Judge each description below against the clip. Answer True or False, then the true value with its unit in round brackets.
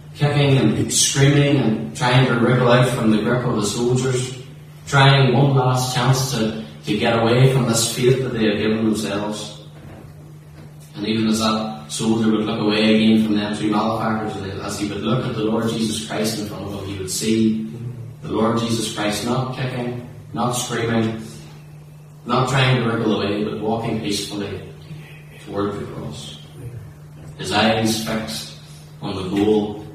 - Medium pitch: False (115 Hz)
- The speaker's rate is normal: True (170 wpm)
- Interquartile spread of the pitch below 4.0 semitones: True (3.3 semitones)